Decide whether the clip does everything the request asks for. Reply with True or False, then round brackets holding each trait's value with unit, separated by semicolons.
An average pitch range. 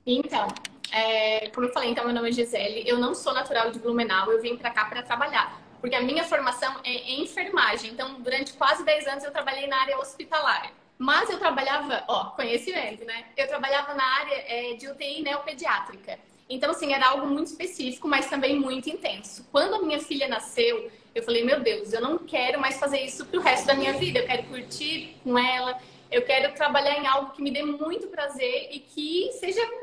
True (3.7 semitones)